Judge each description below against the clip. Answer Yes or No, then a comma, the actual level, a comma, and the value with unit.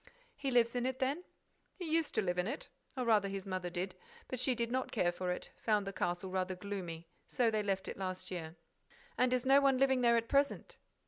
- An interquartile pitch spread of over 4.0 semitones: Yes, wide, 5.6 semitones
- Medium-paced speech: No, fast, 230 wpm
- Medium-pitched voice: No, high, 215 Hz